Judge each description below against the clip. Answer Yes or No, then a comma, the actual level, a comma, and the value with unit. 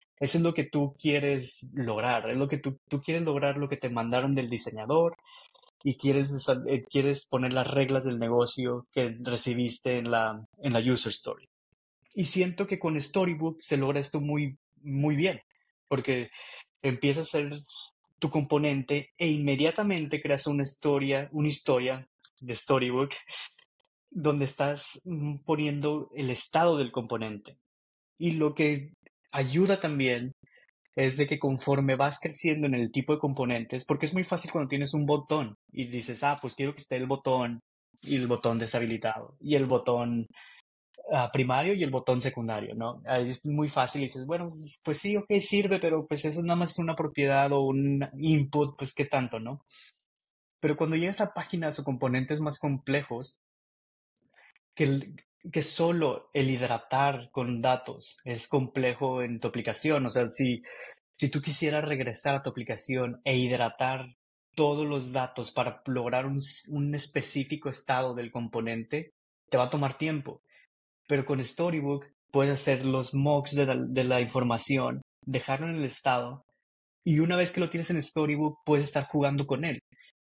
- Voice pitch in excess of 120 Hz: Yes, medium, 140 Hz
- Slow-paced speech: No, average, 165 wpm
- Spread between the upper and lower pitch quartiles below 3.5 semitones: Yes, average, 2.9 semitones